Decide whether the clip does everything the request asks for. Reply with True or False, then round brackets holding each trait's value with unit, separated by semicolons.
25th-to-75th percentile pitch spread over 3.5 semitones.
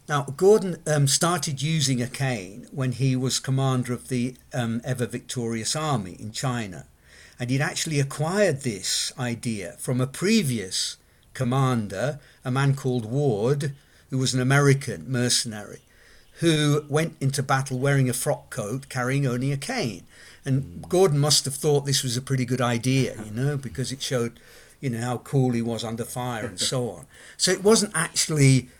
False (2.8 semitones)